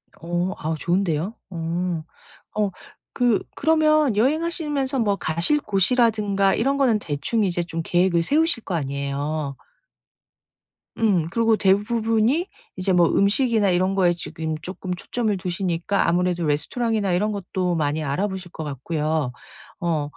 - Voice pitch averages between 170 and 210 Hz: Yes, high, 190 Hz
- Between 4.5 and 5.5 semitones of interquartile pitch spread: Yes, average, 5.2 semitones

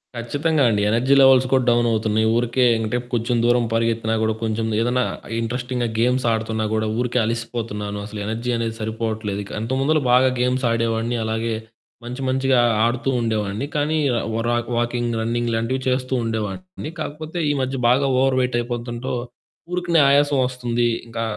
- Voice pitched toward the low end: Yes, low, 120 Hz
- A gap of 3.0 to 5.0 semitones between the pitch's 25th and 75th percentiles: No, narrow, 2.4 semitones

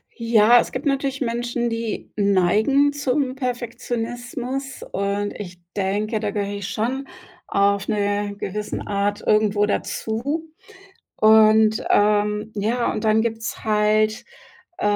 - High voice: Yes, high, 220 Hz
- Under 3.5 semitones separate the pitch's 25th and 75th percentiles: Yes, average, 2.7 semitones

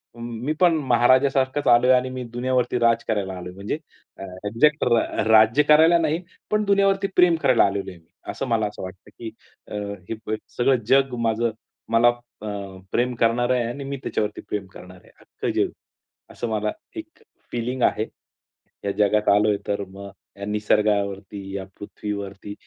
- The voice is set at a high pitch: No, low, 115 Hz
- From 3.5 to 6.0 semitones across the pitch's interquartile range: Yes, average, 3.9 semitones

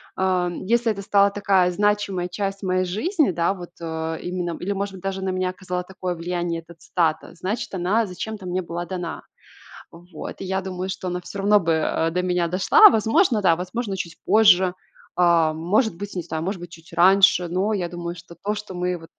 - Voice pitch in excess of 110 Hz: Yes, medium, 185 Hz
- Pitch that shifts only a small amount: Yes, narrow, 2.3 semitones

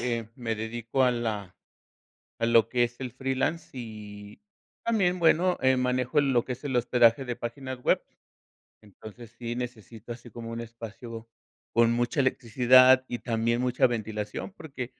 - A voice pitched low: Yes, low, 120 Hz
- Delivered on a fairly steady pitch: Yes, narrow, 2.1 semitones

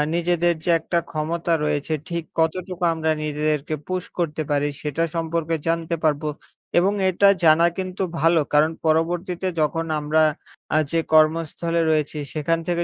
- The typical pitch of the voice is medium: Yes, medium, 165 Hz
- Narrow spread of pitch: Yes, narrow, 1.8 semitones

